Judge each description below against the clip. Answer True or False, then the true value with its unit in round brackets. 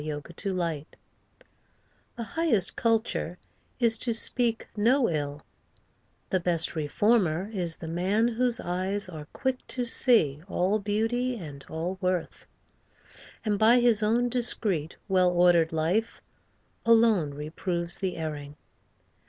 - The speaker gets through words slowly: True (120 wpm)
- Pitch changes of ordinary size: False (5.7 semitones)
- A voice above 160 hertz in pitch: True (190 Hz)